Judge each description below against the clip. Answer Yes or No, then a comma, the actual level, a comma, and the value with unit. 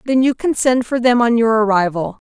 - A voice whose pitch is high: Yes, high, 235 Hz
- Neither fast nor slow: No, fast, 235 wpm